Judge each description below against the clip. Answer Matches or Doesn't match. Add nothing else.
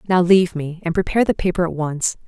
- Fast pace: Matches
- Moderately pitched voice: Matches